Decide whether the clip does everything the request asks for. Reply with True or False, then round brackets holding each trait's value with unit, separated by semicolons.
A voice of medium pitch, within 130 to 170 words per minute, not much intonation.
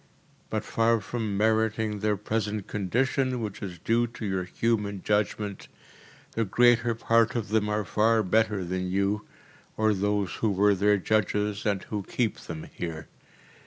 False (105 Hz; 155 wpm; 2.2 semitones)